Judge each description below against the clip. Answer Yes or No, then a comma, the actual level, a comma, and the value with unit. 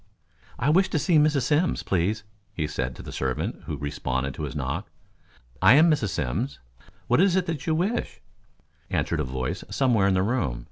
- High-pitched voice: No, low, 105 Hz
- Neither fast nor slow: Yes, average, 185 wpm